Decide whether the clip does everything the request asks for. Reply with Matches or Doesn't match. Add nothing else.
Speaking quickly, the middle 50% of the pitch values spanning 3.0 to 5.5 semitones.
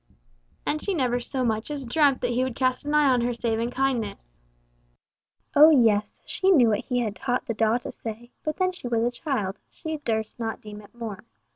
Matches